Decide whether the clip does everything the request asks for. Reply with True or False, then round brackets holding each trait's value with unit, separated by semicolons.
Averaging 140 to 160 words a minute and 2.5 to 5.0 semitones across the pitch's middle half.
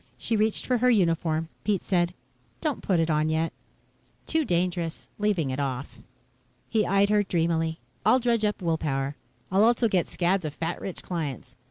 False (175 wpm; 4.5 semitones)